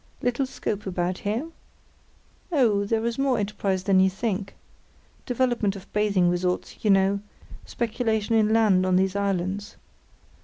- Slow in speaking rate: Yes, slow, 130 wpm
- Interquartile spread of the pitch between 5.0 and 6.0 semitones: No, average, 3.0 semitones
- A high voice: Yes, high, 205 Hz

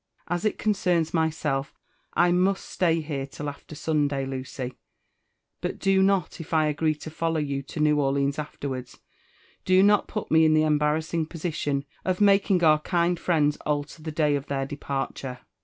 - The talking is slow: No, average, 175 wpm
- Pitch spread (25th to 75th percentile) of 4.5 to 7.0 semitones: No, average, 3.3 semitones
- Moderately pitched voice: Yes, medium, 155 Hz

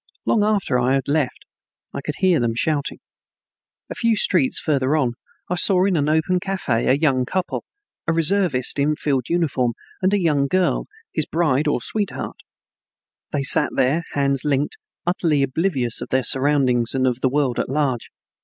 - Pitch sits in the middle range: Yes, medium, 145 Hz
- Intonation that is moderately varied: Yes, average, 4.8 semitones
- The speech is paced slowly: No, average, 175 wpm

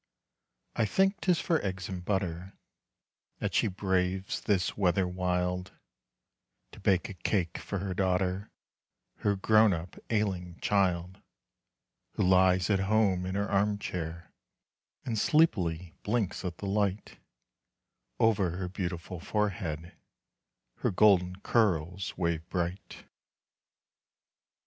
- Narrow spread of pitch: Yes, narrow, 2.2 semitones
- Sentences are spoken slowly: Yes, slow, 115 wpm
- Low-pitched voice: Yes, very low, 95 Hz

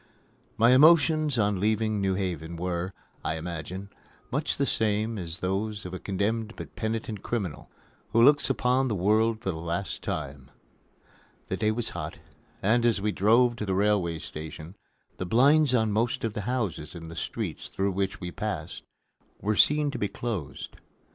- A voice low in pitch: Yes, low, 105 Hz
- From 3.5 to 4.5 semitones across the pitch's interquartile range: Yes, average, 4.2 semitones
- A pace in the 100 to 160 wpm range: No, average, 170 wpm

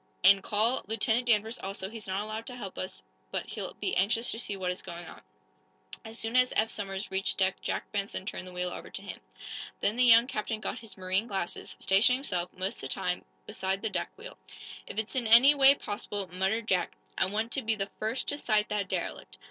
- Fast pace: Yes, fast, 220 wpm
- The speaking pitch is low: No, high, 210 Hz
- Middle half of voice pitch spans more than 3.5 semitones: No, average, 3.2 semitones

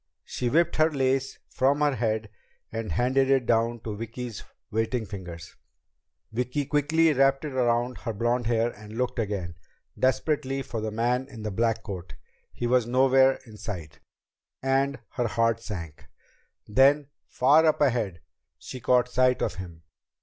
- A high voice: No, low, 120 Hz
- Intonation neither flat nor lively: Yes, average, 3.4 semitones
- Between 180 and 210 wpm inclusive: No, average, 155 wpm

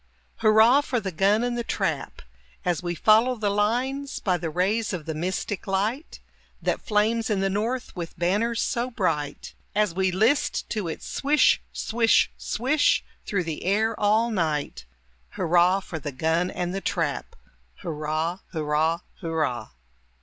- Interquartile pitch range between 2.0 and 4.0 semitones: No, average, 5.2 semitones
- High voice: Yes, high, 195 Hz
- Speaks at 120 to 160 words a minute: Yes, average, 150 wpm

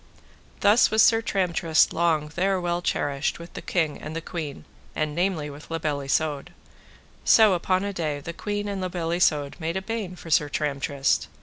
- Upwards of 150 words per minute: Yes, average, 190 wpm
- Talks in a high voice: No, medium, 170 Hz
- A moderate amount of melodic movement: Yes, average, 3.9 semitones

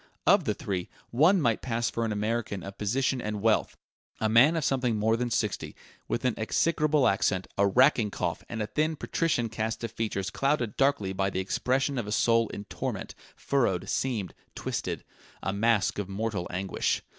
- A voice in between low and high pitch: No, low, 115 Hz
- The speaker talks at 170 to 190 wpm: Yes, average, 185 wpm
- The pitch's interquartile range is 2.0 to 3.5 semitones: No, average, 4.2 semitones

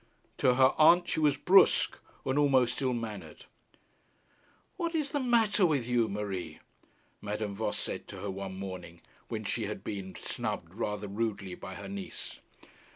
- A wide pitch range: Yes, wide, 6.7 semitones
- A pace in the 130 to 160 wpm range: Yes, average, 155 wpm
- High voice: No, low, 110 Hz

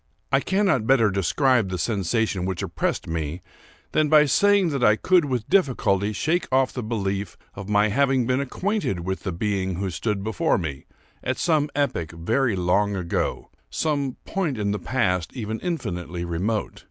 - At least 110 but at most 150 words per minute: No, average, 165 wpm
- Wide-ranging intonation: Yes, wide, 6.5 semitones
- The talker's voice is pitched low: Yes, low, 110 Hz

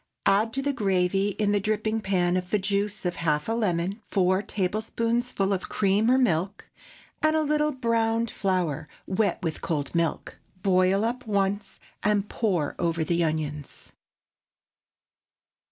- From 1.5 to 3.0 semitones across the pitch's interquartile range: No, average, 3.8 semitones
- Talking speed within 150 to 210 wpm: No, average, 140 wpm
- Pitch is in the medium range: No, high, 200 Hz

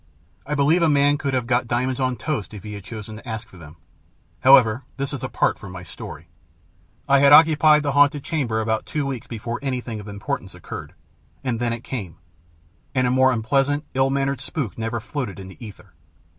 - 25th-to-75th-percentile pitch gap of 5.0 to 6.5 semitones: No, average, 4.1 semitones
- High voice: No, low, 125 Hz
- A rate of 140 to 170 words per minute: No, average, 200 wpm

